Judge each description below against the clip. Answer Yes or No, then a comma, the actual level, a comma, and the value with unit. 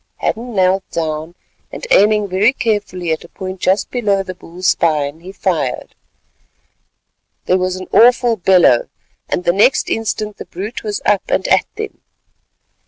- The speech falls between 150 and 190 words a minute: Yes, average, 155 wpm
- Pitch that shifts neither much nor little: Yes, average, 3.3 semitones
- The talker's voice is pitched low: No, high, 190 Hz